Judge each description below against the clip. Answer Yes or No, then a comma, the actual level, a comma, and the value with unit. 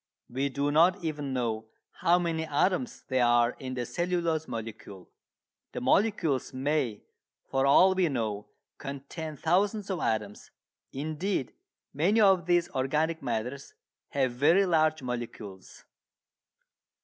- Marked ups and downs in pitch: Yes, wide, 5.7 semitones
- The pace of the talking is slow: Yes, slow, 125 wpm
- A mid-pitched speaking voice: Yes, medium, 145 Hz